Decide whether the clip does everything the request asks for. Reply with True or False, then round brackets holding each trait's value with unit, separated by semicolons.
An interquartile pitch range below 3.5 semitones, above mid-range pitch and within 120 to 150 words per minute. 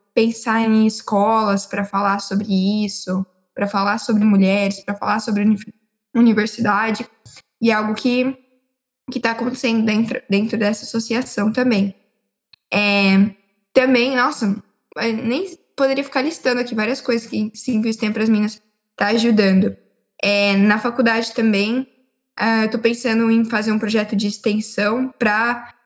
True (2.8 semitones; 220 Hz; 135 wpm)